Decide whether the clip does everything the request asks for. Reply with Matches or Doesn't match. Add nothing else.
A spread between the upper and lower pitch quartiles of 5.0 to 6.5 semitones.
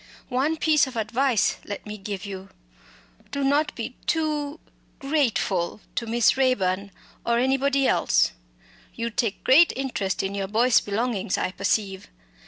Matches